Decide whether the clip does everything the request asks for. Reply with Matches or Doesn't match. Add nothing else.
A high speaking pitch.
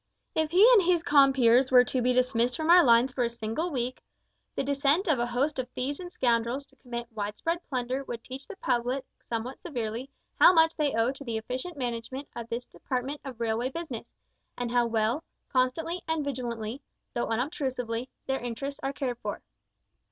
Matches